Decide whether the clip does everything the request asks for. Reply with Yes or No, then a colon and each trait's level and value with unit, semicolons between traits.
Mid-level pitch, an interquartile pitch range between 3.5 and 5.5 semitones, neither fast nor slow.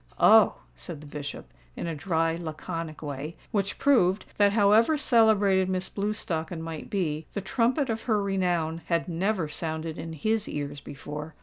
Yes: medium, 175 Hz; average, 4.5 semitones; average, 160 wpm